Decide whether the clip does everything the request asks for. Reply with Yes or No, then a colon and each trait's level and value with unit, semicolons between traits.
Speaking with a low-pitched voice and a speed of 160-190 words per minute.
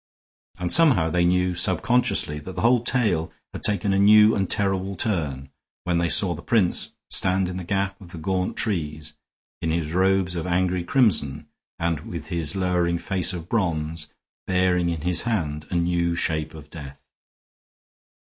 Yes: very low, 90 Hz; average, 170 wpm